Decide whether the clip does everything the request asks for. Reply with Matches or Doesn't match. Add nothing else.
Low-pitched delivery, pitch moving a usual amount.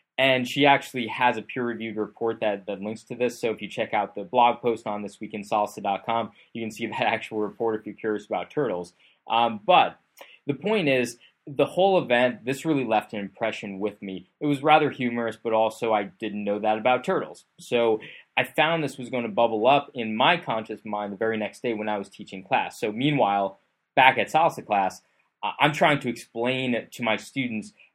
Matches